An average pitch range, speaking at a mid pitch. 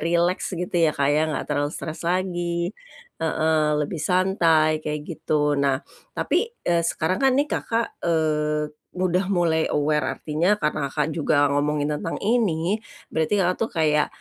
Yes: average, 3.1 semitones; medium, 160 Hz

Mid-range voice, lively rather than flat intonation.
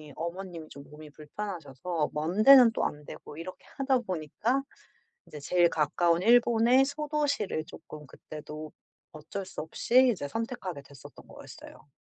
Yes: medium, 175 Hz; wide, 7.4 semitones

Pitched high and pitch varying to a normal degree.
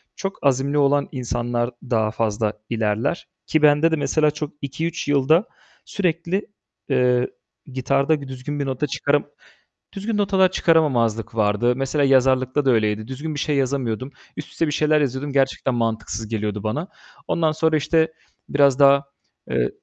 No: medium, 140 Hz; average, 3.9 semitones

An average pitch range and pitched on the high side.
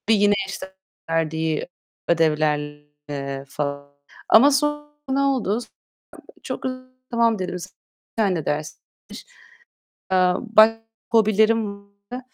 No: wide, 6.9 semitones; high, 195 Hz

